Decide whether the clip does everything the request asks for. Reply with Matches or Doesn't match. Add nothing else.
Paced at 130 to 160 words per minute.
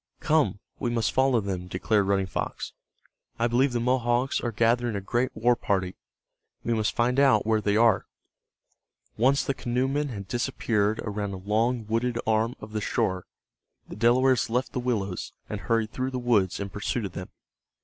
Doesn't match